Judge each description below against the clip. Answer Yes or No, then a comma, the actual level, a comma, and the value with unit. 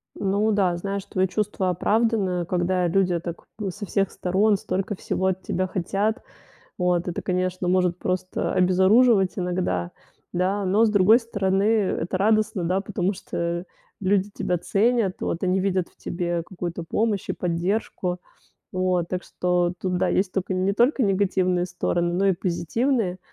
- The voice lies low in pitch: No, medium, 185 Hz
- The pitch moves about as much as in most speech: No, narrow, 2.1 semitones